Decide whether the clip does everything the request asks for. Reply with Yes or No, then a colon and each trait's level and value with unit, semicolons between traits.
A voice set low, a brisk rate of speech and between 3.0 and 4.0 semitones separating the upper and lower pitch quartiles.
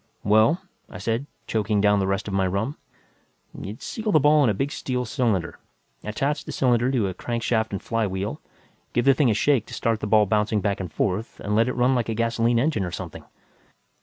Yes: low, 110 Hz; fast, 215 wpm; average, 3.6 semitones